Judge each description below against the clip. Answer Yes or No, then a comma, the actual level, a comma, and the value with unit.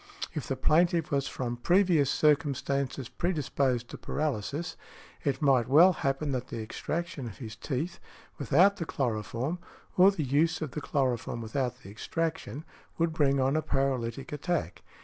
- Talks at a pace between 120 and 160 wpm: Yes, average, 155 wpm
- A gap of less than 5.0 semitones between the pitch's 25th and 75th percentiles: Yes, average, 4.2 semitones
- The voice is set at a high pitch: No, medium, 140 Hz